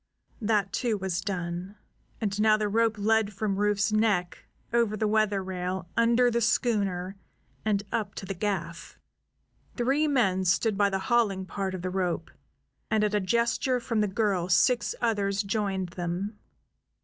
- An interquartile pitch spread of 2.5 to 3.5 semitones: Yes, average, 2.8 semitones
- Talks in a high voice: Yes, high, 205 Hz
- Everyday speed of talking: Yes, average, 160 wpm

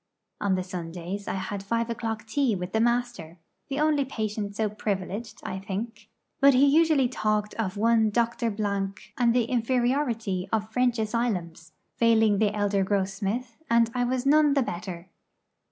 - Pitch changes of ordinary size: Yes, average, 3.4 semitones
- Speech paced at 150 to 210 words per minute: Yes, average, 160 wpm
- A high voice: Yes, high, 220 Hz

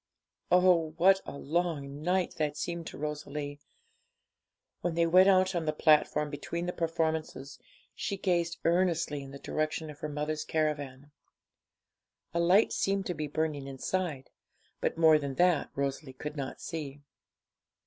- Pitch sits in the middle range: Yes, medium, 155 Hz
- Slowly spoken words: No, average, 150 wpm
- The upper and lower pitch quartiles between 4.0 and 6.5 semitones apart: No, average, 3.0 semitones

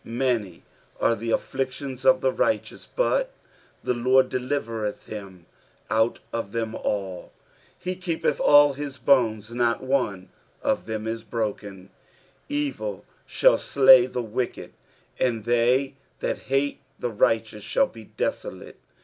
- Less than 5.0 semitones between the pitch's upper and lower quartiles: Yes, average, 3.5 semitones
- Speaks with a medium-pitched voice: No, low, 120 Hz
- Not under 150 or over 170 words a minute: No, average, 140 wpm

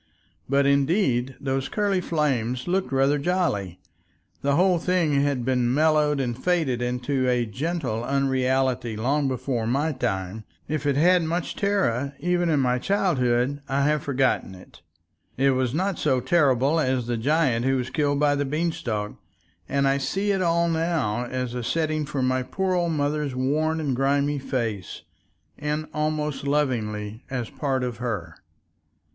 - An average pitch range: Yes, average, 3.7 semitones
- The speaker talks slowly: No, average, 160 wpm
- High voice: No, medium, 140 Hz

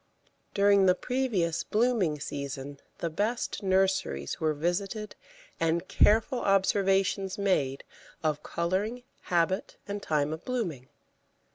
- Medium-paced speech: No, slow, 110 wpm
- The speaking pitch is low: No, high, 190 Hz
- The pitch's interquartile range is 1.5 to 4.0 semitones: No, average, 4.5 semitones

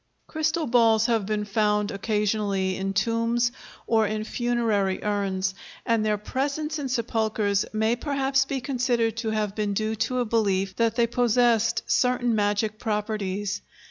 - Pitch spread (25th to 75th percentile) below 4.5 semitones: Yes, narrow, 2.6 semitones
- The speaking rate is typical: Yes, average, 145 wpm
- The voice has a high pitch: Yes, high, 220 Hz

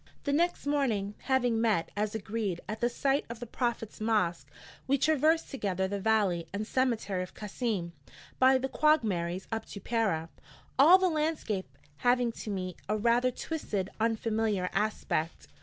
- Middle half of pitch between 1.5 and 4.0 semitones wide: No, average, 4.8 semitones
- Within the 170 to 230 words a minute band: No, average, 155 wpm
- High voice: Yes, high, 225 Hz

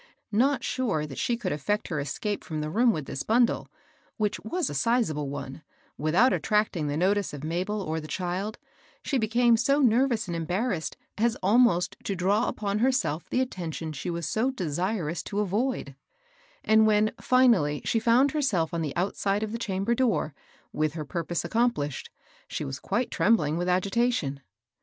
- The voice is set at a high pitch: Yes, high, 200 Hz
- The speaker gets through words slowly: No, average, 180 wpm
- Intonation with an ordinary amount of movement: No, wide, 6.6 semitones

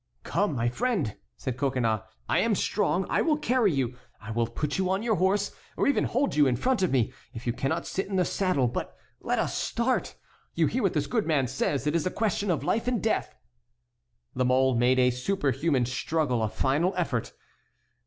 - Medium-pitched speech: Yes, medium, 150 Hz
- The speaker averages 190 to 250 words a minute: Yes, fast, 205 wpm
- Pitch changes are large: Yes, wide, 7.9 semitones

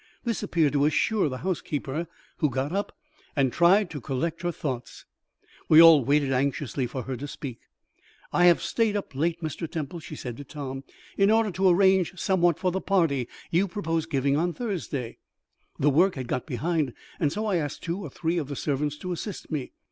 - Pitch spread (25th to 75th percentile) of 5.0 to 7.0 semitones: No, average, 4.4 semitones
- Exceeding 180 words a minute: Yes, average, 195 wpm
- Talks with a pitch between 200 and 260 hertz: No, medium, 160 Hz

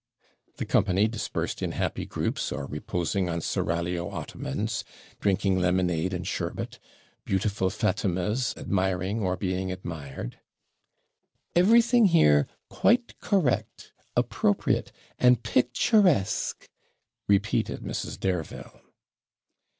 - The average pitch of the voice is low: Yes, very low, 95 Hz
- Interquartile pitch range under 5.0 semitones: Yes, average, 4.6 semitones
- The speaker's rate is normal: No, slow, 95 wpm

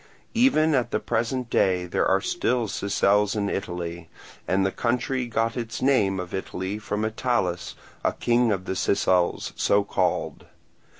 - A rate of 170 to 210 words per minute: No, average, 155 wpm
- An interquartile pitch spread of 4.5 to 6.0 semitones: No, average, 4.1 semitones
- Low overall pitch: Yes, low, 105 Hz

